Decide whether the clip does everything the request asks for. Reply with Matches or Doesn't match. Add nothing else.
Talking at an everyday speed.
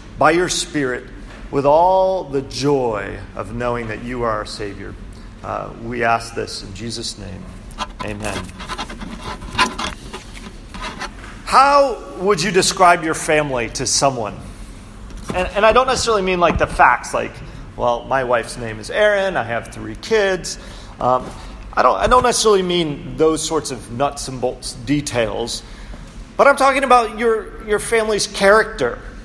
Matches